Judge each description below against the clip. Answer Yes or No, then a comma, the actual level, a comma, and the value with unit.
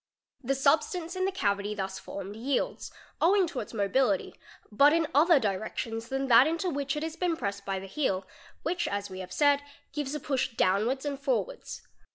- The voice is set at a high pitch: Yes, very high, 270 Hz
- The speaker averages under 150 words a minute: No, average, 190 wpm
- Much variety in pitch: Yes, wide, 7.1 semitones